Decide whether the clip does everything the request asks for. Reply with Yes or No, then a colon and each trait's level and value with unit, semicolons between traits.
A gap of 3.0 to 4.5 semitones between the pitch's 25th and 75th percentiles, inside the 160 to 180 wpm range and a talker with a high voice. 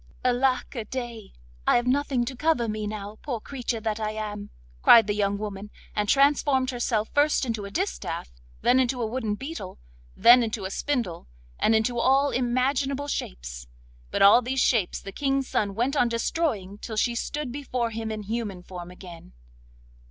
Yes: average, 3.9 semitones; average, 175 wpm; high, 230 Hz